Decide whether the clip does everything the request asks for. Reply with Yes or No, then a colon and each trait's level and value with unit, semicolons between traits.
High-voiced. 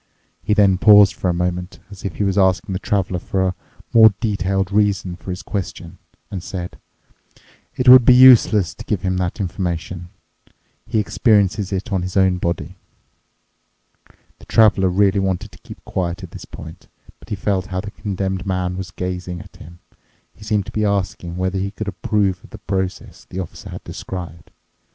No: very low, 95 Hz